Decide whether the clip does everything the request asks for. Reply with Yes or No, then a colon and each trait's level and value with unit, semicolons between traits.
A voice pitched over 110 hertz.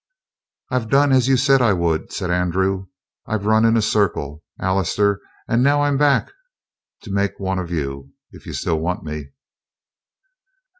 No: low, 100 Hz